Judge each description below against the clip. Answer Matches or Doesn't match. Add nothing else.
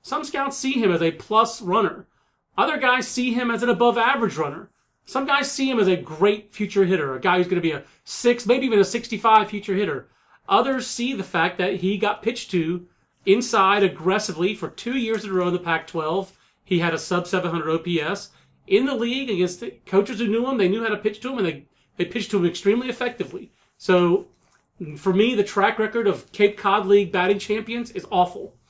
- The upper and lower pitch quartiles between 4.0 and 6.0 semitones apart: Matches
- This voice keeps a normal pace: Doesn't match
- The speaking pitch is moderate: Doesn't match